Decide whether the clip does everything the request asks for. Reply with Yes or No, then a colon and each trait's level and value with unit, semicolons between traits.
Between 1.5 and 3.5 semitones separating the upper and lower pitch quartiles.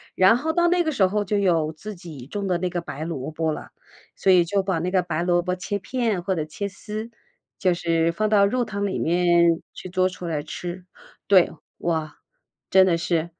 Yes: average, 3.2 semitones